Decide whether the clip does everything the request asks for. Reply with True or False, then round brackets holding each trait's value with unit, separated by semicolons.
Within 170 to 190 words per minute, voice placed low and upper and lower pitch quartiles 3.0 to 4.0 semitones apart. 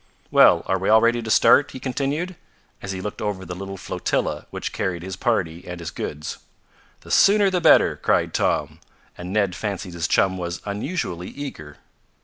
False (180 wpm; 95 Hz; 5.2 semitones)